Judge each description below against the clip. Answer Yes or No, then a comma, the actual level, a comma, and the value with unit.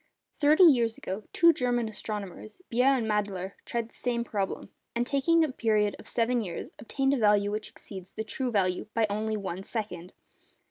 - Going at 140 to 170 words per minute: No, average, 180 wpm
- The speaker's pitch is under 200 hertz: No, high, 220 Hz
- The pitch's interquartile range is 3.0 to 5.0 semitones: Yes, average, 3.3 semitones